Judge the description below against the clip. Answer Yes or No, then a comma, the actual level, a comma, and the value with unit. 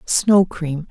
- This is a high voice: No, medium, 175 Hz